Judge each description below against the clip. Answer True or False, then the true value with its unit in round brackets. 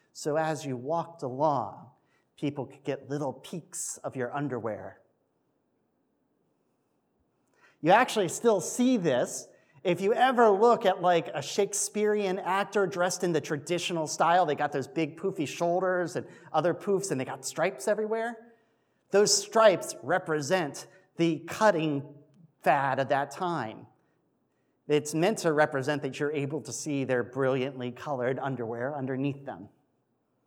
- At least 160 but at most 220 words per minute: False (140 wpm)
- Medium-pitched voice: True (160 Hz)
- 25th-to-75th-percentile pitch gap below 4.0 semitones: False (5.2 semitones)